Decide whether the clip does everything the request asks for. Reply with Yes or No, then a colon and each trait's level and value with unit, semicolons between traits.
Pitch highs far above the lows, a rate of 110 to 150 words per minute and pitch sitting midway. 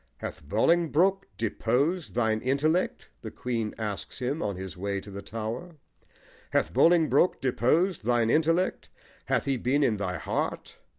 No: wide, 7.1 semitones; average, 140 wpm; low, 125 Hz